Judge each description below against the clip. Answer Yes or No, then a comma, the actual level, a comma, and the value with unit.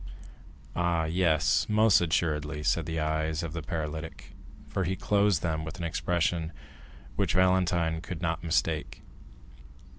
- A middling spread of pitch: No, narrow, 2.0 semitones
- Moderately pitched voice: No, very low, 80 Hz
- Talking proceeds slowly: Yes, slow, 130 wpm